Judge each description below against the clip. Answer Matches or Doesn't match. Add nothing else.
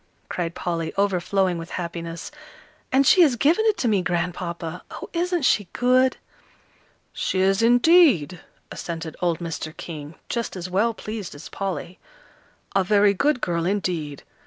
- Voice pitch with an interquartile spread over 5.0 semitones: Matches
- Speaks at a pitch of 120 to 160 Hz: Doesn't match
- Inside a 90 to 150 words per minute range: Matches